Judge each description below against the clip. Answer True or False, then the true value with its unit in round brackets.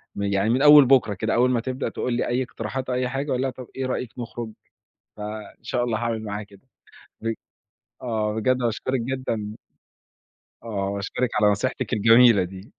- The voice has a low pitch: True (115 Hz)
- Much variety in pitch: False (3.2 semitones)